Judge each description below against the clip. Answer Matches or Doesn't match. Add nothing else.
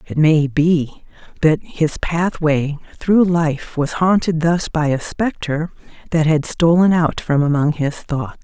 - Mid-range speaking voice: Matches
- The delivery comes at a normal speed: Matches